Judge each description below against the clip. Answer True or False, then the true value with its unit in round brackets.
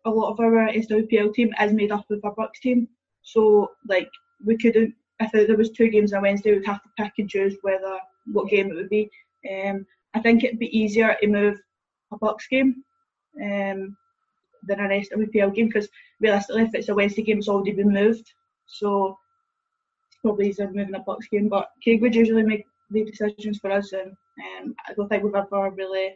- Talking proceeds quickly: True (215 wpm)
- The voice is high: True (215 Hz)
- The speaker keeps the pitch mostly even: True (2.3 semitones)